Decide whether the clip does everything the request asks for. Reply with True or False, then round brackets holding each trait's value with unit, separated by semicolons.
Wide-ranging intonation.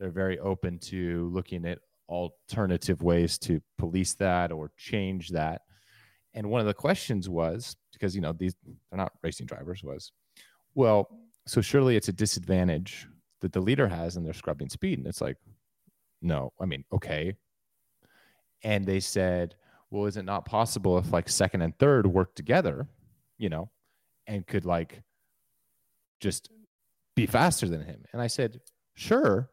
False (4.1 semitones)